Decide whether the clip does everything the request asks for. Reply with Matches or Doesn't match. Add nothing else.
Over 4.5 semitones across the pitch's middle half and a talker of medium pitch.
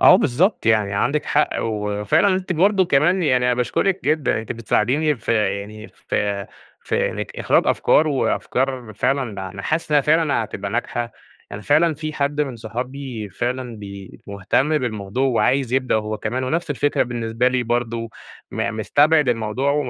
Doesn't match